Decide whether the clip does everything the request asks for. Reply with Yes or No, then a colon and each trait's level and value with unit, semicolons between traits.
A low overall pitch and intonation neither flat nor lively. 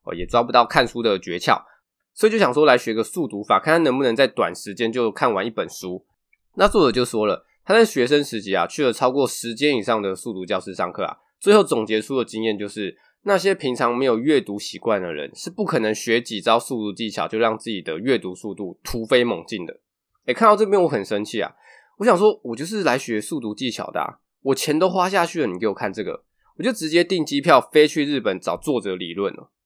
No: low, 115 Hz; wide, 6.3 semitones